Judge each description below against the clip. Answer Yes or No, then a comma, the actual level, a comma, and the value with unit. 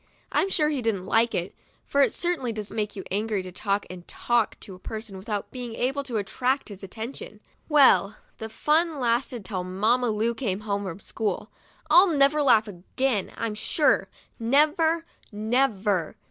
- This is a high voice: Yes, high, 225 Hz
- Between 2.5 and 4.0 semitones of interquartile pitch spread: No, average, 5.0 semitones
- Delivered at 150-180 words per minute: Yes, average, 170 wpm